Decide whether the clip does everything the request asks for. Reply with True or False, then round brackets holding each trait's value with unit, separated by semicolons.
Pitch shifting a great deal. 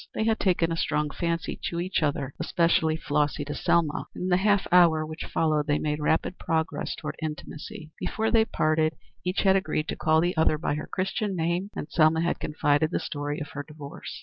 False (2.8 semitones)